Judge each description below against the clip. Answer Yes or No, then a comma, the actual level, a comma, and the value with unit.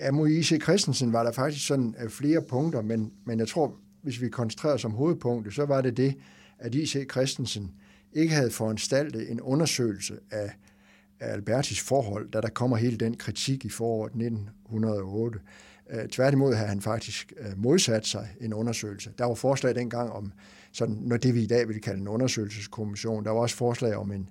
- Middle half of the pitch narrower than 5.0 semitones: Yes, average, 3.4 semitones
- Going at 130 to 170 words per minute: No, average, 180 wpm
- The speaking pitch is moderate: No, low, 115 Hz